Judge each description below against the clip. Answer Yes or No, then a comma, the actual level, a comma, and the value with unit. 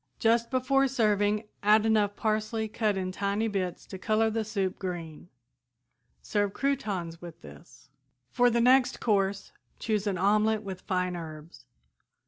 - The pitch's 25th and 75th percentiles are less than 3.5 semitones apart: Yes, average, 3.0 semitones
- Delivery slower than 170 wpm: Yes, average, 140 wpm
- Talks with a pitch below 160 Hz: No, high, 210 Hz